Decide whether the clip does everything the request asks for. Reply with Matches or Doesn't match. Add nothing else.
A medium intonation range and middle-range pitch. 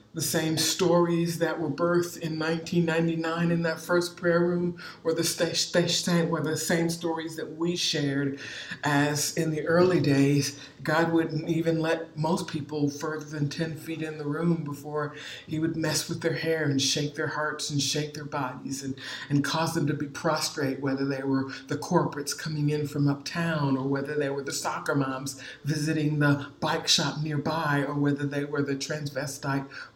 Doesn't match